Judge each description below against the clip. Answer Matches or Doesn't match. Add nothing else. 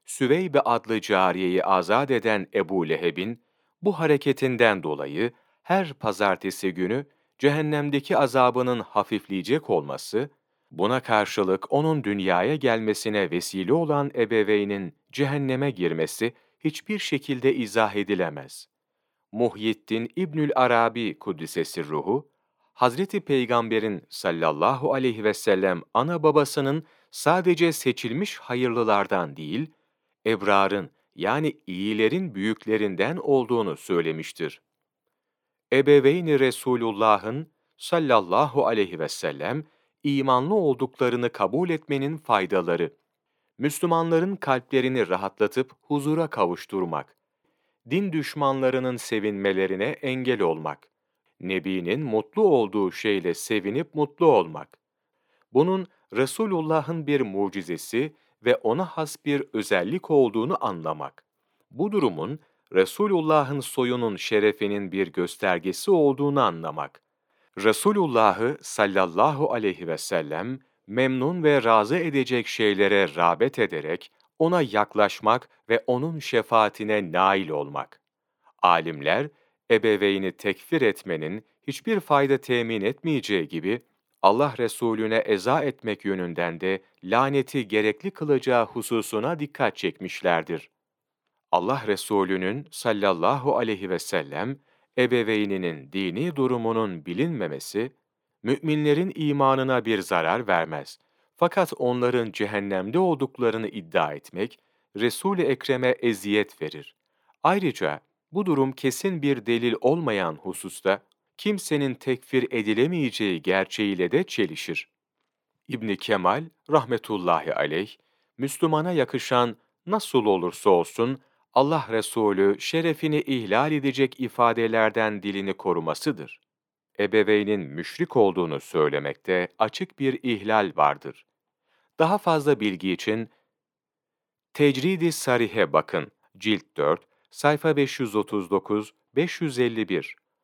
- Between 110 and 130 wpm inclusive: Doesn't match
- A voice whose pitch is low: Matches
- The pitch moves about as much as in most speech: Doesn't match